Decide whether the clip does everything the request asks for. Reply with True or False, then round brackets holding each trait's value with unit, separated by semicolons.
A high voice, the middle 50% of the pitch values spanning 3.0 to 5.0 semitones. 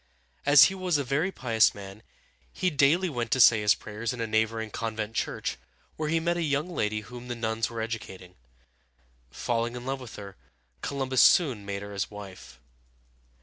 False (115 Hz; 4.7 semitones)